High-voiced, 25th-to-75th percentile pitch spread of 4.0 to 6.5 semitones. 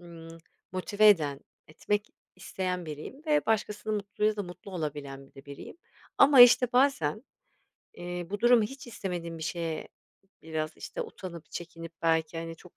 No: medium, 175 Hz; average, 4.6 semitones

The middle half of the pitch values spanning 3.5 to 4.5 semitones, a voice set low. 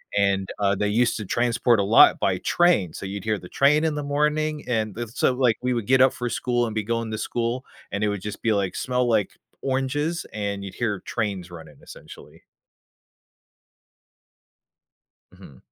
Yes: average, 4.1 semitones; low, 115 Hz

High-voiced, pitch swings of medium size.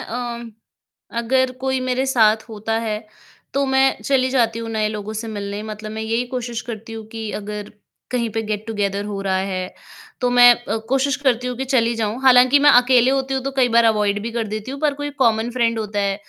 Yes: high, 230 Hz; average, 3.1 semitones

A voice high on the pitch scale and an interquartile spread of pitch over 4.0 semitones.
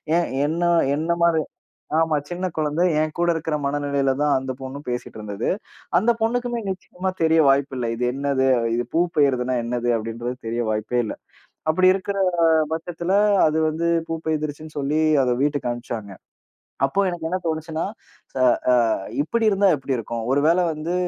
No: medium, 155 Hz; average, 4.6 semitones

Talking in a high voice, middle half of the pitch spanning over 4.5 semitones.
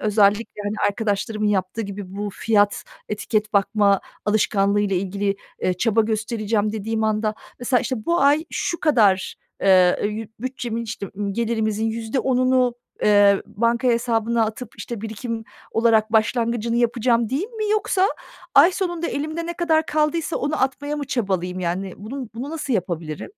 No: high, 225 Hz; average, 3.8 semitones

